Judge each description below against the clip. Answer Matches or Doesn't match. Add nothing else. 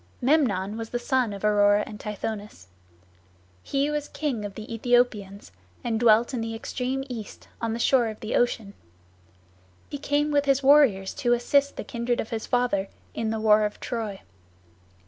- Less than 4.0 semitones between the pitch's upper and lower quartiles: Matches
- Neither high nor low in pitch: Doesn't match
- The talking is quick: Doesn't match